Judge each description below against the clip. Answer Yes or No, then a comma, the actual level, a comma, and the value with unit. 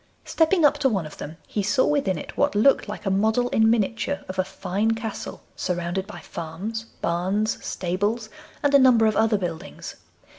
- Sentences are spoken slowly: No, average, 185 wpm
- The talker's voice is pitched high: Yes, high, 215 Hz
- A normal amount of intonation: Yes, average, 3.9 semitones